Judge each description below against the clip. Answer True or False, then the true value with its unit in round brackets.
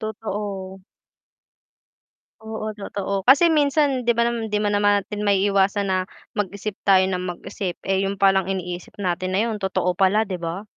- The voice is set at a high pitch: True (200 Hz)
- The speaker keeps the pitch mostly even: True (2.2 semitones)